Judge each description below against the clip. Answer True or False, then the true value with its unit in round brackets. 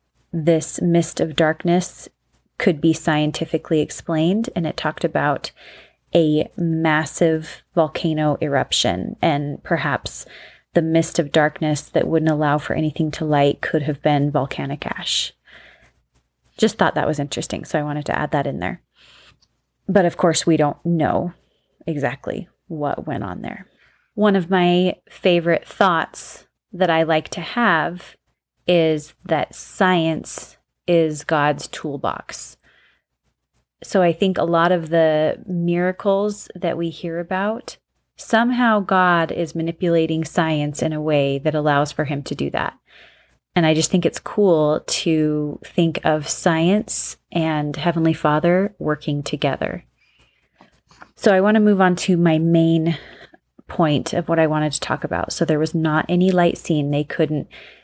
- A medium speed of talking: True (145 wpm)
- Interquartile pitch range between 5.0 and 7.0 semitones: False (2.5 semitones)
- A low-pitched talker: False (165 Hz)